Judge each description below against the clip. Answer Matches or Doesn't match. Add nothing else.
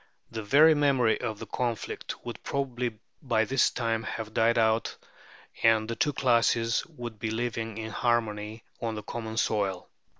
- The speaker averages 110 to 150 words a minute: Doesn't match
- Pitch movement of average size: Doesn't match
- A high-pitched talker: Doesn't match